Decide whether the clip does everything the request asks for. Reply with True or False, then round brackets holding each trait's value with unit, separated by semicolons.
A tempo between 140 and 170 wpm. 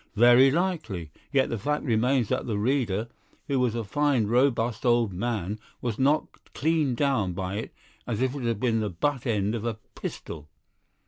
False (180 wpm)